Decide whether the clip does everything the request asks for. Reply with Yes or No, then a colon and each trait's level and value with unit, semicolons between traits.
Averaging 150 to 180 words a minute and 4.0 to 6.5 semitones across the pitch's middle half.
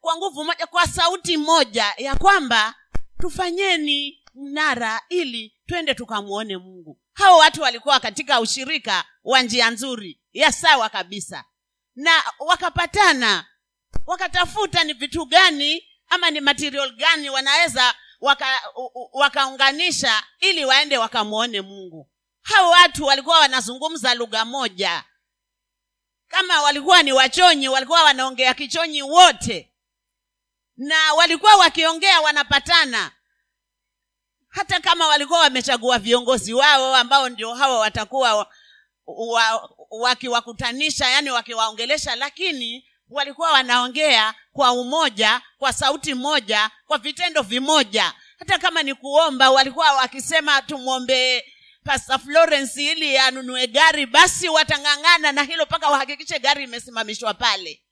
No: average, 105 wpm; average, 4.7 semitones